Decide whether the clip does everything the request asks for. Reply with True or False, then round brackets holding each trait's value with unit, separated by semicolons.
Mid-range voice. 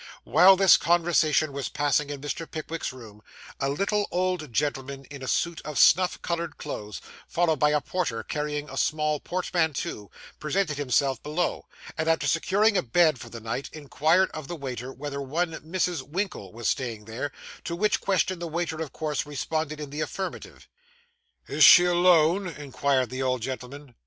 True (150 Hz)